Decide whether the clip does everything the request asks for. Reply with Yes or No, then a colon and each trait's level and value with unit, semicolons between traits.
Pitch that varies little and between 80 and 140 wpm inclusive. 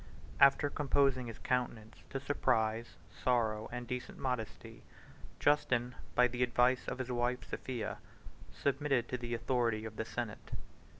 Yes: narrow, 1.9 semitones; slow, 135 wpm